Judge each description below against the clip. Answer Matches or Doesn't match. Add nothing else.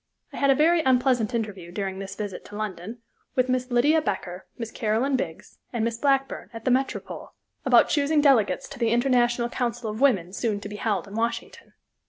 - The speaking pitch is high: Matches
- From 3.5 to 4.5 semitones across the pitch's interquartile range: Matches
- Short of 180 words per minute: Doesn't match